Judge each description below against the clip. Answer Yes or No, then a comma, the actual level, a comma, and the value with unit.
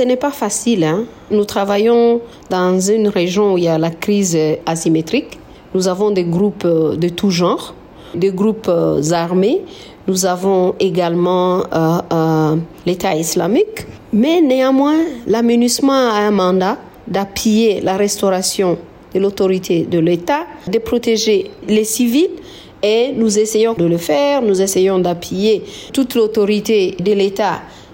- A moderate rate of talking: No, slow, 135 wpm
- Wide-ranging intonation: No, average, 4.2 semitones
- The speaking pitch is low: No, high, 200 Hz